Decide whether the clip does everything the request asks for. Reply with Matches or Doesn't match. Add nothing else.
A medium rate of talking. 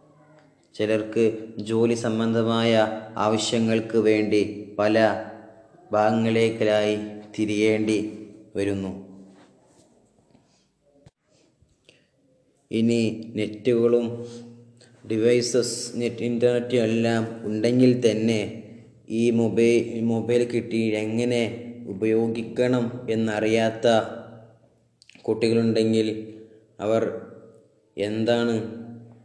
Doesn't match